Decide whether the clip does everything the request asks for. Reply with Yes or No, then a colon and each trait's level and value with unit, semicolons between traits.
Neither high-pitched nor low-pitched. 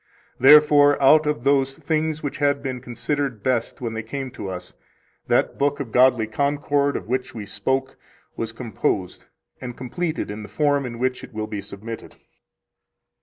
No: low, 130 Hz